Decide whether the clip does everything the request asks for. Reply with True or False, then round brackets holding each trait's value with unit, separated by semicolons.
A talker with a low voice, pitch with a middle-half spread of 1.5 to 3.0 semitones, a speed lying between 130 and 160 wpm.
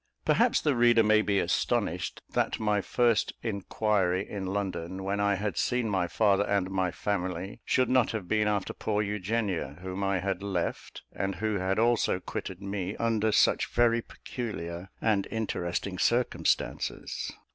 True (100 Hz; 2.7 semitones; 155 wpm)